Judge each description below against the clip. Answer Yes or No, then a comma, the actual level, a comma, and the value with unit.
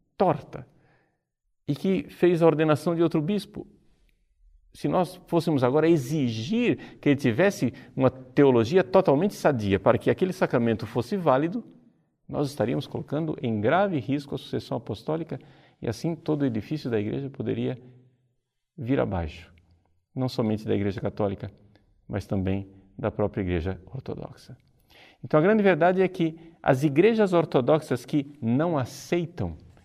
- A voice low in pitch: Yes, low, 130 Hz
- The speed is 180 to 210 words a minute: No, average, 140 wpm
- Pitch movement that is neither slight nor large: No, wide, 7.0 semitones